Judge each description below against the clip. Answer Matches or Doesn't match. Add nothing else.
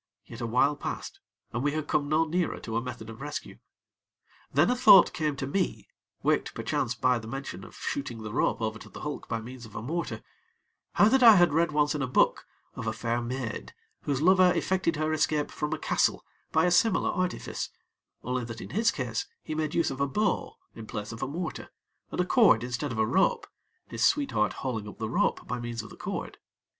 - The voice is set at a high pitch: Doesn't match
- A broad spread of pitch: Matches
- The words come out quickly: Matches